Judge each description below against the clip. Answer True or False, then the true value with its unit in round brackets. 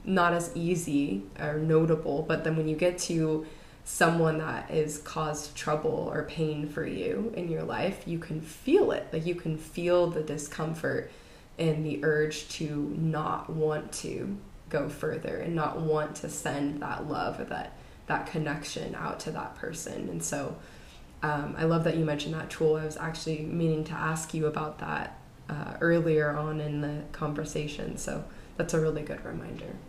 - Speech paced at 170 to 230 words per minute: True (175 wpm)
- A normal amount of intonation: False (1.4 semitones)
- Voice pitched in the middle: True (155 Hz)